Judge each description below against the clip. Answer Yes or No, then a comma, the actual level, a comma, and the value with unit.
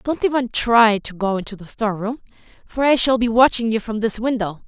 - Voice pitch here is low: No, high, 225 Hz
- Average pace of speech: No, fast, 220 wpm